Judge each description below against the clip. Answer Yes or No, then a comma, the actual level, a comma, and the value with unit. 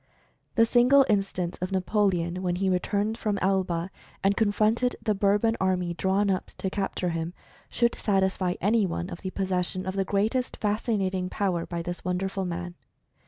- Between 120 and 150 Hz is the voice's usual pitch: No, high, 190 Hz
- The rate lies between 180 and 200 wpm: No, average, 165 wpm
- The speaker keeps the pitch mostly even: Yes, narrow, 2.3 semitones